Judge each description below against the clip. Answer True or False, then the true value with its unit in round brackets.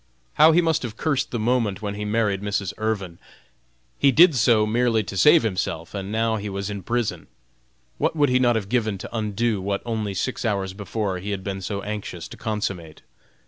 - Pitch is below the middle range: True (105 Hz)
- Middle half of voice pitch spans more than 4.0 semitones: False (3.2 semitones)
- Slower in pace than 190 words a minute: False (200 wpm)